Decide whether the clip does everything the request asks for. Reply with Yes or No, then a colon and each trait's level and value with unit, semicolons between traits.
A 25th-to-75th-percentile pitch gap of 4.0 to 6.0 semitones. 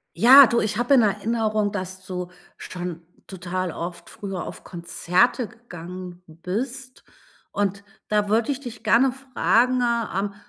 Yes: average, 4.8 semitones